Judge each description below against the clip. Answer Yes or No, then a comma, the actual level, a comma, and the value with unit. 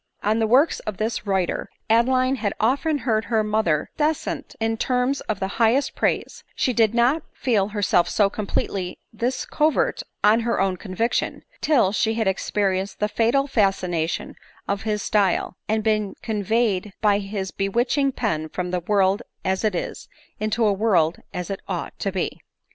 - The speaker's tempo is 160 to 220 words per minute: Yes, average, 170 wpm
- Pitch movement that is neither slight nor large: Yes, average, 3.4 semitones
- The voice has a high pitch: Yes, high, 215 Hz